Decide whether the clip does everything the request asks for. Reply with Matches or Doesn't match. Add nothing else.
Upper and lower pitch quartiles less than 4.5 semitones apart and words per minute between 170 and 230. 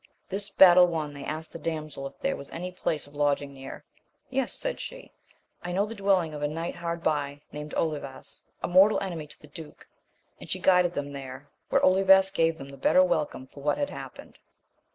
Matches